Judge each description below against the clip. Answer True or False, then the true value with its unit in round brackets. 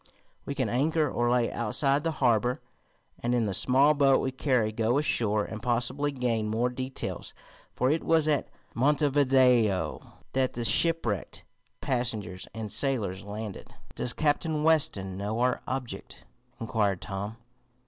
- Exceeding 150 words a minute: False (140 wpm)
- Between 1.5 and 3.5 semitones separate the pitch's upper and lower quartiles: False (4.2 semitones)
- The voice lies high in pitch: False (125 Hz)